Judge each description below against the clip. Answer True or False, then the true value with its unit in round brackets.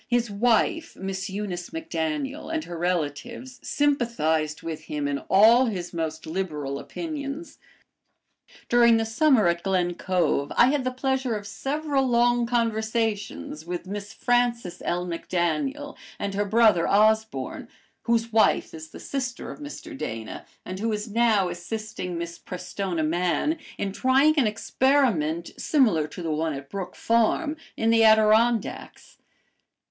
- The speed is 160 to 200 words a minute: False (140 wpm)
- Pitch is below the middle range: False (215 Hz)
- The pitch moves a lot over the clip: True (5.9 semitones)